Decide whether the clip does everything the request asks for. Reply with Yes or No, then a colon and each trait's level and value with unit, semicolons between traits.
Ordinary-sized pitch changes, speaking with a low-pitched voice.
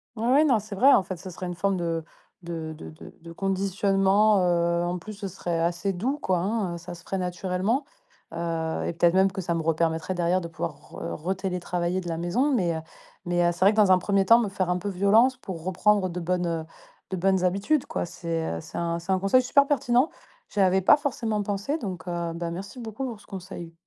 No: average, 3.1 semitones; medium, 185 Hz